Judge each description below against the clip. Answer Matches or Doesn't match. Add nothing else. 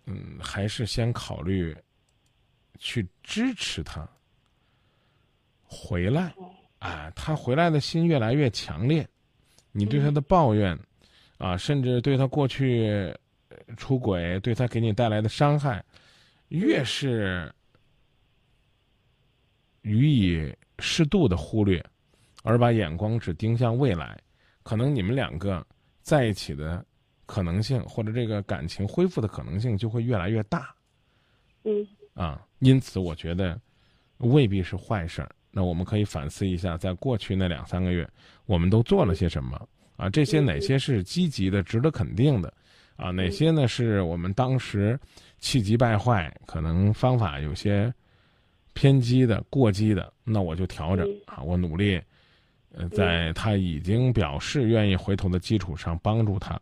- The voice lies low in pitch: Matches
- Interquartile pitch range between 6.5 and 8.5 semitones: Doesn't match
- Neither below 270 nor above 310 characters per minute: Doesn't match